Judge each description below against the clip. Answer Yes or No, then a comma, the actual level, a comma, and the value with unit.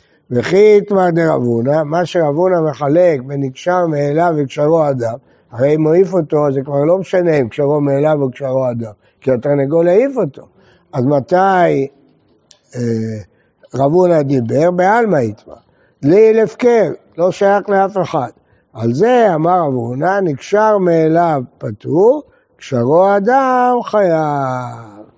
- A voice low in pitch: No, medium, 160 Hz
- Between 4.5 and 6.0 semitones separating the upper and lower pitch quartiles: Yes, average, 5.2 semitones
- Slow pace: No, average, 135 wpm